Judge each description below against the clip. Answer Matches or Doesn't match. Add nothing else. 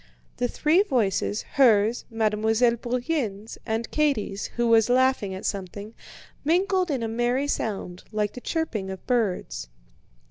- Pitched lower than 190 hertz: Doesn't match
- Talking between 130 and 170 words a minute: Matches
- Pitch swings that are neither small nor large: Matches